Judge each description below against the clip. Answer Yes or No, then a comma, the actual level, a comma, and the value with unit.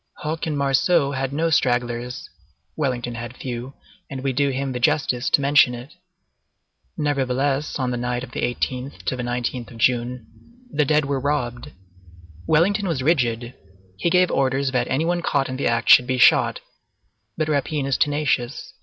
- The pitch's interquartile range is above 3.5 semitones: No, average, 3.0 semitones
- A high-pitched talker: No, low, 135 Hz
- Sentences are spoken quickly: No, average, 170 wpm